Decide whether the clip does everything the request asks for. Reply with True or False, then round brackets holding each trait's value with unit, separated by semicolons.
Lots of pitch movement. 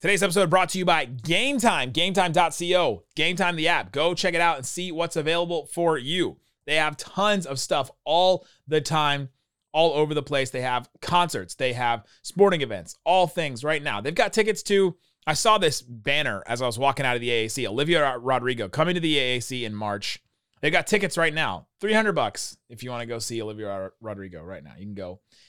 True (6.0 semitones)